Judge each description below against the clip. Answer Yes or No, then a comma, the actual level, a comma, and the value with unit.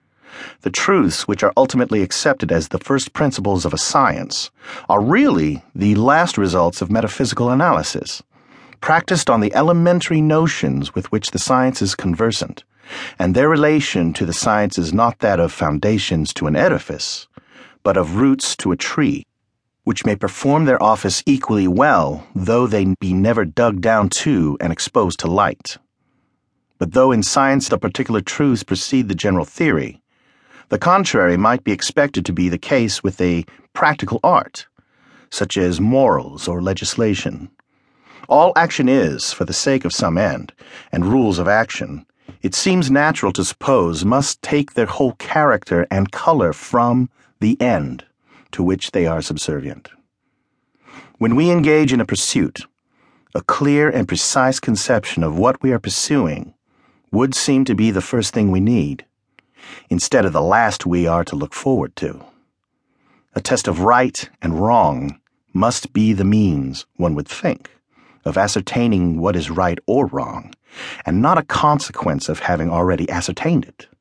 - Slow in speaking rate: No, average, 160 wpm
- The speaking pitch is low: Yes, low, 105 Hz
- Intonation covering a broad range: Yes, wide, 6.5 semitones